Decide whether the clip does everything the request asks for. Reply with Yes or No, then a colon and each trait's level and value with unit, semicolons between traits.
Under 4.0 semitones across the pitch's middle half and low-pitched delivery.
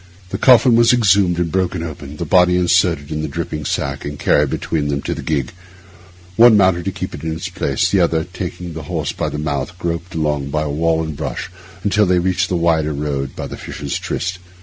Yes: average, 3.4 semitones; very low, 85 Hz